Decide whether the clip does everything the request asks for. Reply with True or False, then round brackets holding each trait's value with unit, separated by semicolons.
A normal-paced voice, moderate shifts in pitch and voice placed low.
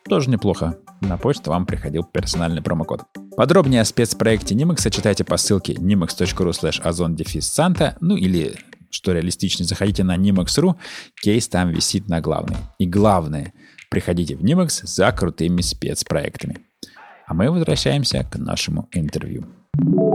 True (130 wpm; 4.8 semitones; 95 Hz)